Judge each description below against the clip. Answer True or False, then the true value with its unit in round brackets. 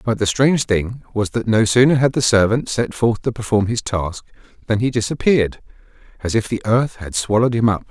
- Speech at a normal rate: False (215 wpm)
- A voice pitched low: True (110 Hz)